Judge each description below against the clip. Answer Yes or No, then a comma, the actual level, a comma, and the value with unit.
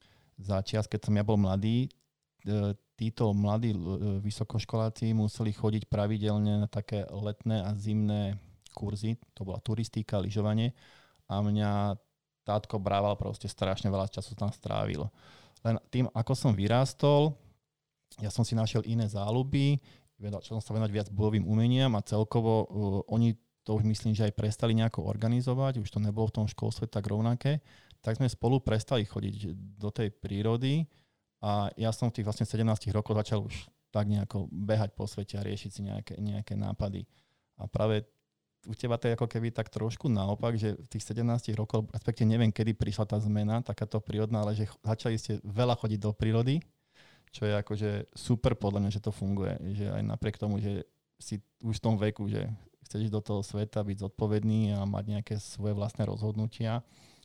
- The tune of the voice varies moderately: No, narrow, 1.8 semitones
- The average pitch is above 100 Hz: Yes, low, 110 Hz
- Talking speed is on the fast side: Yes, fast, 170 wpm